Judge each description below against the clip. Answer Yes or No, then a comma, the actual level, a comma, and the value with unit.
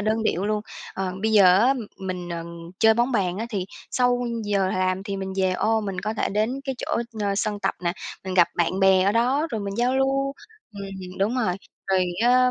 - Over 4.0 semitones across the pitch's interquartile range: No, average, 3.7 semitones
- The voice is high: Yes, high, 200 Hz